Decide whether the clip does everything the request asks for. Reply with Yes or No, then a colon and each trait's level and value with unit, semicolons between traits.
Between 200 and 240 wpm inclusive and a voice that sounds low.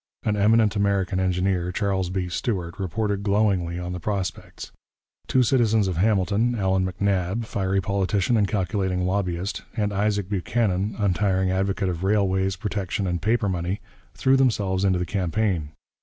No: average, 145 wpm; very low, 95 Hz